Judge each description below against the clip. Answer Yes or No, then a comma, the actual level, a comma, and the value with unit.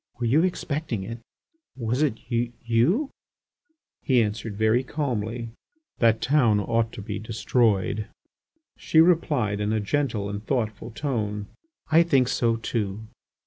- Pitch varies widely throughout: No, average, 4.1 semitones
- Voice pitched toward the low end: Yes, low, 115 Hz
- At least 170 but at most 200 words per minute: No, slow, 135 wpm